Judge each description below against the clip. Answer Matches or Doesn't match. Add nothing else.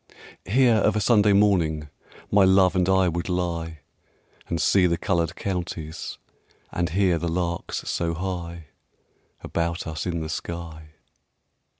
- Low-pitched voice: Matches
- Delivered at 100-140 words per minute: Matches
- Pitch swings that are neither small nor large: Doesn't match